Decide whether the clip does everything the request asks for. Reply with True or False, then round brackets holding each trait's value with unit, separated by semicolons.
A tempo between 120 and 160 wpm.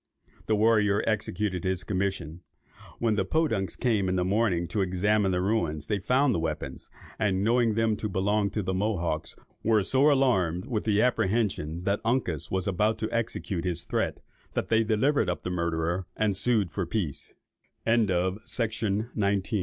True (155 wpm)